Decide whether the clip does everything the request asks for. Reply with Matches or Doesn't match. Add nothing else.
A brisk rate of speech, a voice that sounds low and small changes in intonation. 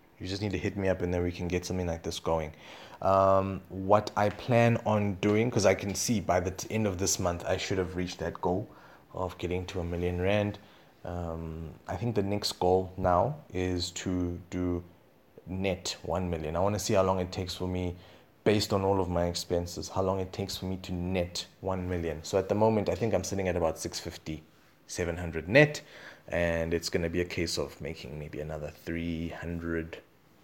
Matches